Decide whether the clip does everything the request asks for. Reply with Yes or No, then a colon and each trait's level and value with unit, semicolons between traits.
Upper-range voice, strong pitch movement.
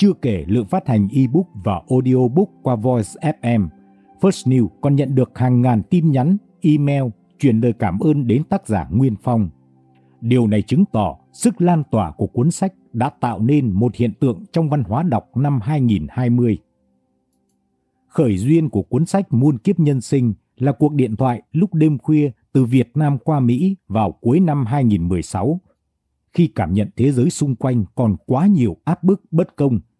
No: low, 125 Hz; wide, 6.0 semitones